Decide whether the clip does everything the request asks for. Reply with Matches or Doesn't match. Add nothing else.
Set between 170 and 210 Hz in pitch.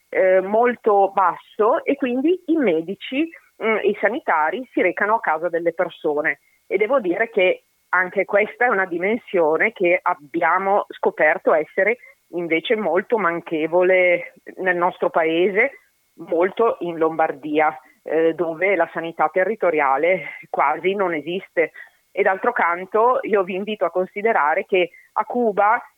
Matches